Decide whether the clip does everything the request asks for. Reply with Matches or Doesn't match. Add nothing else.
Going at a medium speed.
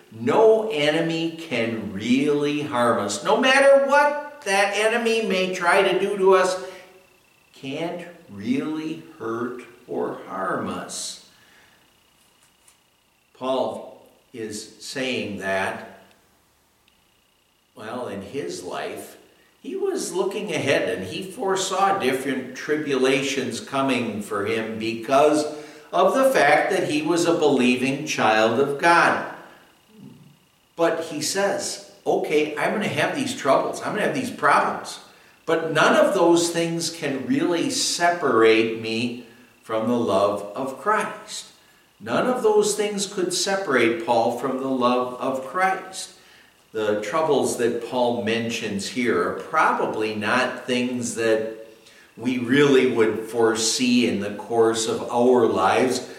Doesn't match